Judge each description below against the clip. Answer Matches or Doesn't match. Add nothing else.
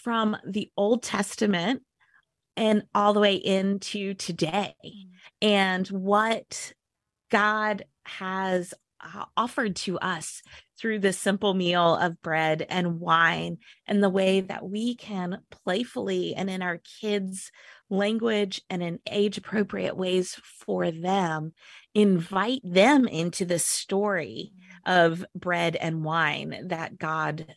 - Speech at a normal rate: Doesn't match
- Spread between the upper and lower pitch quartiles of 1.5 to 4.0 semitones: Matches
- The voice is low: Doesn't match